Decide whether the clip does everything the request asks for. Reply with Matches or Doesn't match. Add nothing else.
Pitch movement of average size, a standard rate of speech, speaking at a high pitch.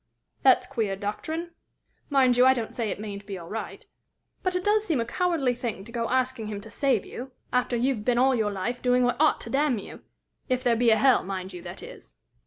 Doesn't match